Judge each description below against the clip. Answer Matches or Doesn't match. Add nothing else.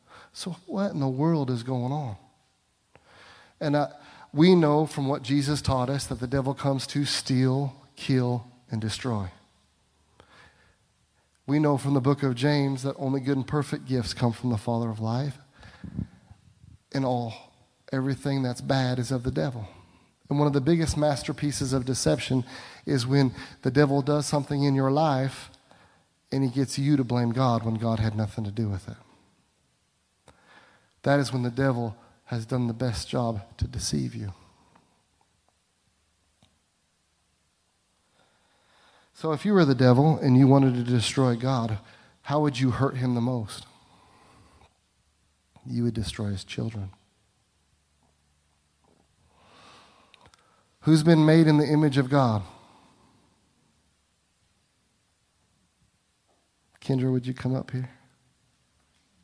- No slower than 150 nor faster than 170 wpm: Doesn't match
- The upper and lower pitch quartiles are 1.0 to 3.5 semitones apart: Doesn't match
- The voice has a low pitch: Matches